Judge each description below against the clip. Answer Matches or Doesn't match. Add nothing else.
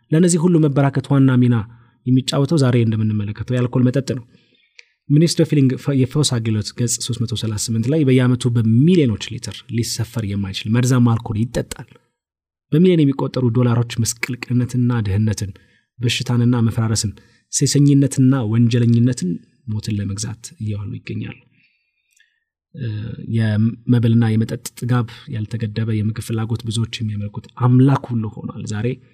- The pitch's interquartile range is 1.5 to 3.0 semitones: Matches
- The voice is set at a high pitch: Doesn't match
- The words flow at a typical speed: Matches